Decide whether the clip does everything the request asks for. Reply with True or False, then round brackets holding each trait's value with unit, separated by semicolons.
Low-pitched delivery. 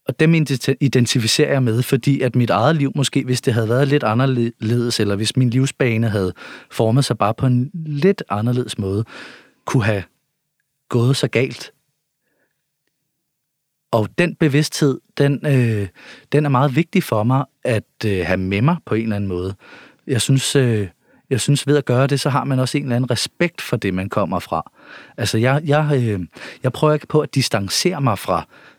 True (130 Hz)